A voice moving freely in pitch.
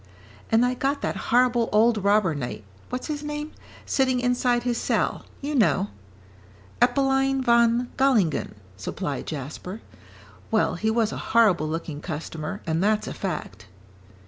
Yes: wide, 5.8 semitones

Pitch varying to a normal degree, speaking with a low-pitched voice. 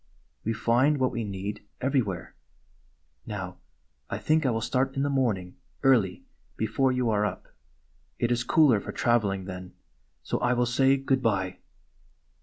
Yes: average, 4.4 semitones; low, 120 Hz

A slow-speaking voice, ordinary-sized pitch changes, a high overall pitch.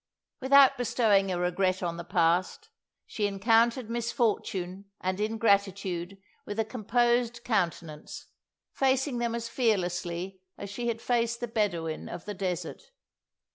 Yes: slow, 130 wpm; average, 4.4 semitones; high, 210 Hz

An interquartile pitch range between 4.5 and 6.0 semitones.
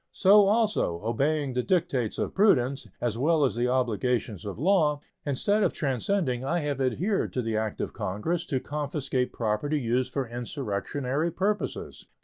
Yes: average, 5.3 semitones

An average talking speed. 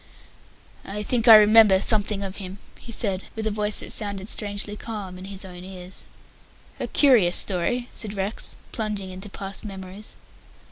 Yes: average, 160 wpm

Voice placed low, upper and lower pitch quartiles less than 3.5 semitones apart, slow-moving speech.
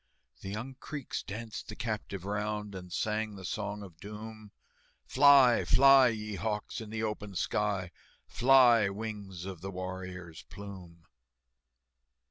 Yes: low, 105 Hz; narrow, 2.6 semitones; slow, 130 wpm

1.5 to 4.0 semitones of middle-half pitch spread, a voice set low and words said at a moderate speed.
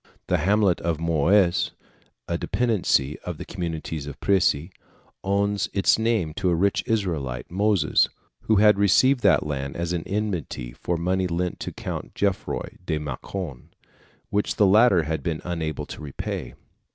No: average, 4.4 semitones; very low, 90 Hz; average, 155 wpm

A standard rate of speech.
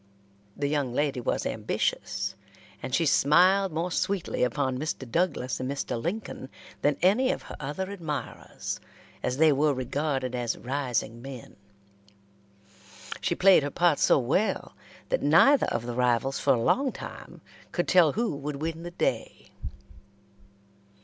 Yes: average, 145 wpm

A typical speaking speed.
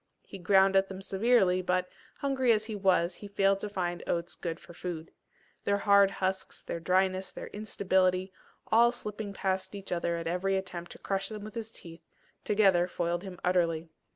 Yes: average, 180 wpm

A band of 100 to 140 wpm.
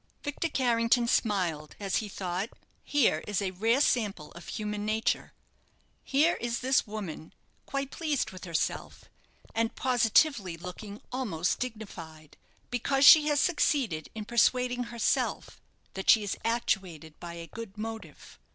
Yes: slow, 135 wpm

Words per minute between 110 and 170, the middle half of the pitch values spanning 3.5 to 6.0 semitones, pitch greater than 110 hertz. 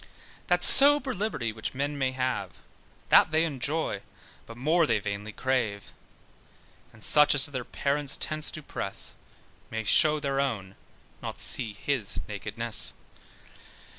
Yes: slow, 135 wpm; average, 5.2 semitones; low, 135 Hz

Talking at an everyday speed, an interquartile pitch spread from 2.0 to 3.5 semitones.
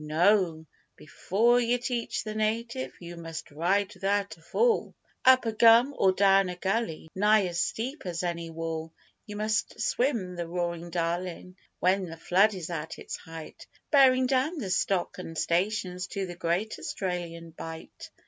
No: average, 160 wpm; average, 4.3 semitones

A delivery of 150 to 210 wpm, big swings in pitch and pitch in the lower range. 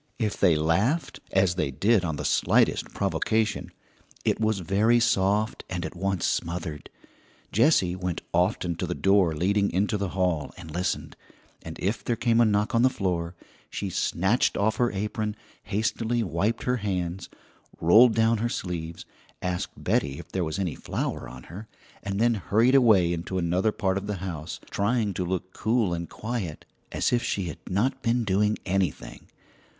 No: average, 170 wpm; average, 3.9 semitones; very low, 95 Hz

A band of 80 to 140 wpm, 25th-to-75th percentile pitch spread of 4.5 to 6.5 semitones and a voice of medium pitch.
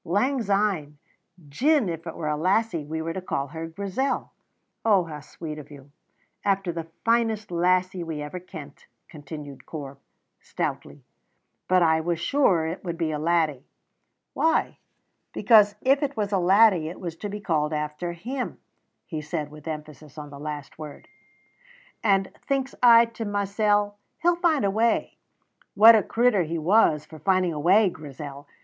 No: average, 165 wpm; average, 5.3 semitones; medium, 175 Hz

